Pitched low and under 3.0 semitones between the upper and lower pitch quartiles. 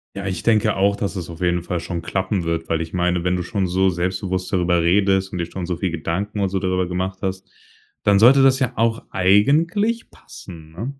Yes: very low, 95 Hz; narrow, 2.6 semitones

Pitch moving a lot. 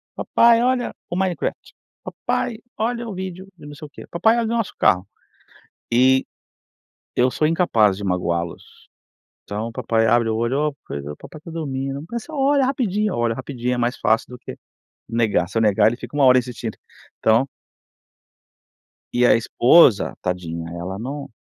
Yes: wide, 8.3 semitones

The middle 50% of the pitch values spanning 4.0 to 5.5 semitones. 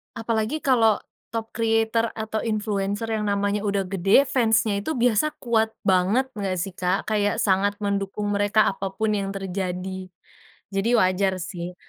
No: narrow, 2.4 semitones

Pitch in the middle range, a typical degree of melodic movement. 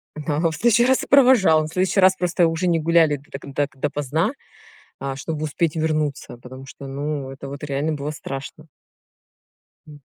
Yes: medium, 155 Hz; average, 3.2 semitones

